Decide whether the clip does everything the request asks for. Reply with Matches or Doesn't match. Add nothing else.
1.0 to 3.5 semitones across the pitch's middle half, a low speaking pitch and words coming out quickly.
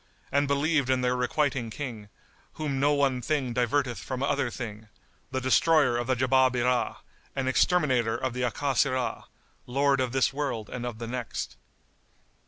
Doesn't match